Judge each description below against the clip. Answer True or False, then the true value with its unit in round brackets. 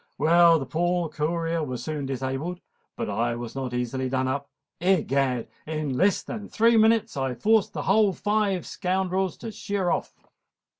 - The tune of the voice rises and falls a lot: True (6.3 semitones)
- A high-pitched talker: False (165 Hz)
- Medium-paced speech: True (160 wpm)